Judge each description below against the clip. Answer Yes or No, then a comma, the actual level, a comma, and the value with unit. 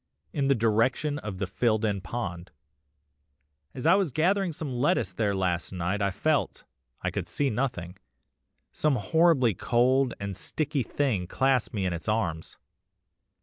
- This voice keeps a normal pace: Yes, average, 150 wpm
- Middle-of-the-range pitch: No, low, 115 Hz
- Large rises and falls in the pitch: Yes, wide, 6.3 semitones